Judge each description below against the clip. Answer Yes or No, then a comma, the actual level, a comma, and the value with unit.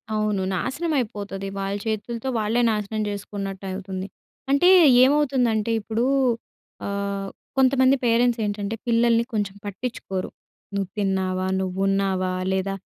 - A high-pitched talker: Yes, high, 205 Hz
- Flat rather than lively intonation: No, average, 3.2 semitones